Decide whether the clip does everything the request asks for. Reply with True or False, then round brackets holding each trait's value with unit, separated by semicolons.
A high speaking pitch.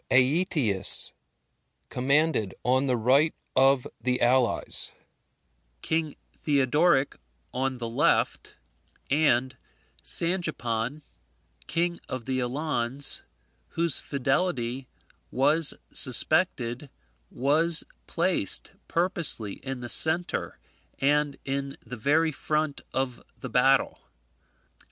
False (135 Hz)